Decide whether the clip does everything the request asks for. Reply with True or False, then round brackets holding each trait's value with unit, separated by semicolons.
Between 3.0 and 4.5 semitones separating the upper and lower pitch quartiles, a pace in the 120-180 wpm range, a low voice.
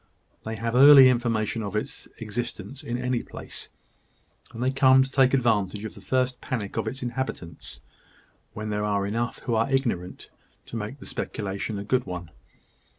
True (3.6 semitones; 170 wpm; 115 Hz)